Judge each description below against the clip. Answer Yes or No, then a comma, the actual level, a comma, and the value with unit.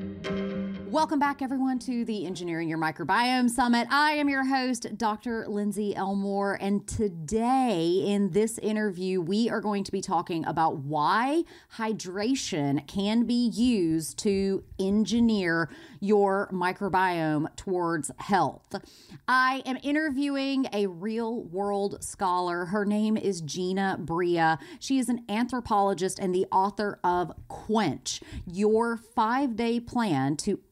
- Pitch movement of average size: Yes, average, 4.2 semitones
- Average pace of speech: No, slow, 125 wpm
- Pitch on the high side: Yes, high, 205 Hz